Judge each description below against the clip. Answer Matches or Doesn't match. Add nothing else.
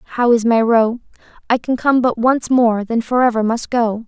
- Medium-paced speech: Doesn't match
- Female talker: Matches